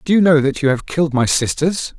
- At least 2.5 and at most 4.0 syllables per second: No, 5.9 syllables/s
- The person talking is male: Yes, male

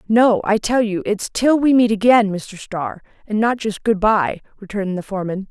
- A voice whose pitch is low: No, high, 210 Hz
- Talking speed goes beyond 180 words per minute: Yes, fast, 205 wpm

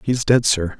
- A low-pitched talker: Yes, low, 110 Hz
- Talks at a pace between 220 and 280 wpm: Yes, fast, 225 wpm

